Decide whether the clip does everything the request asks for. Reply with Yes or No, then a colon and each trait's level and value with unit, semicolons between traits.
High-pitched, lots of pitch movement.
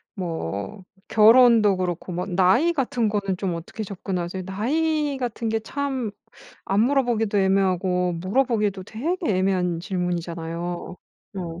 No: high, 195 Hz; average, 4.7 semitones